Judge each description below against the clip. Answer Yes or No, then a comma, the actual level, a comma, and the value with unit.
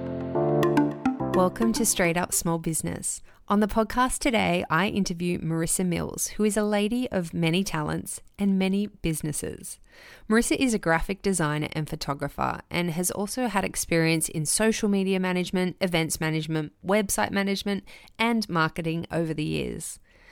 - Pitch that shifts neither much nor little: Yes, average, 4.1 semitones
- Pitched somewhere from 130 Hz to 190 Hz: Yes, medium, 185 Hz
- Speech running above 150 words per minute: No, average, 145 wpm